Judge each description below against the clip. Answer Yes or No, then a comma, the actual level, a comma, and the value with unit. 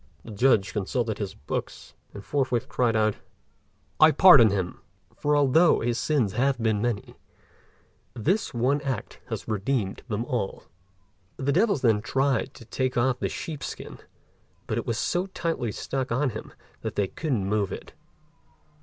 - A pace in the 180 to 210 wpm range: No, average, 155 wpm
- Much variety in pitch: No, average, 4.4 semitones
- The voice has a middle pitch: No, low, 120 Hz